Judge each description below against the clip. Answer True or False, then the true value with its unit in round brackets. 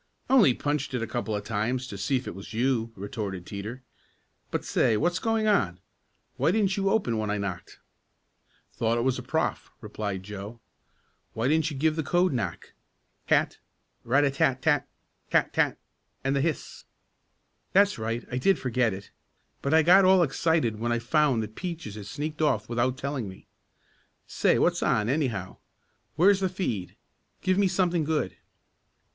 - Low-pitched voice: True (130 Hz)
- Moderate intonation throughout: False (6.5 semitones)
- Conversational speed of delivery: True (175 wpm)